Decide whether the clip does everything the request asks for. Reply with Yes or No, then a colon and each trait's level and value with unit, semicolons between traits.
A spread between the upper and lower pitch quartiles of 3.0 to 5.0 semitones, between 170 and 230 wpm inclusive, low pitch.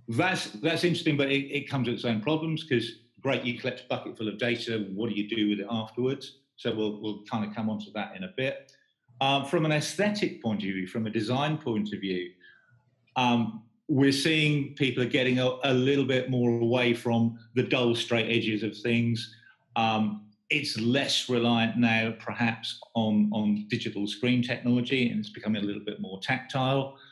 Yes: average, 3.5 semitones; average, 200 wpm; low, 120 Hz